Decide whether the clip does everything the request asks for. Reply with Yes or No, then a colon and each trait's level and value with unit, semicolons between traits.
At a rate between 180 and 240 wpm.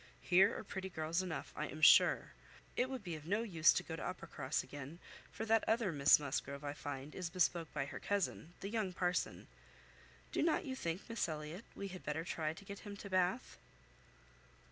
Yes: average, 200 wpm